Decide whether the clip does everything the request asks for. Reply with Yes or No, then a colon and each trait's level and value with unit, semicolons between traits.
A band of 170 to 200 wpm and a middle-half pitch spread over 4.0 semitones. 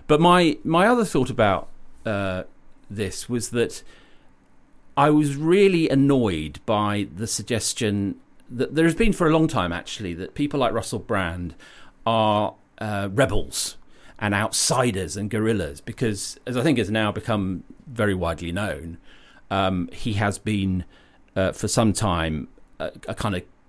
No: average, 150 wpm; wide, 5.6 semitones